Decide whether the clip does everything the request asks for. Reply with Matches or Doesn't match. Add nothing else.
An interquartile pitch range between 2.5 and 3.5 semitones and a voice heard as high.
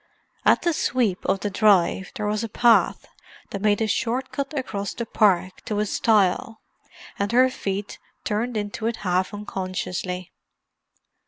Matches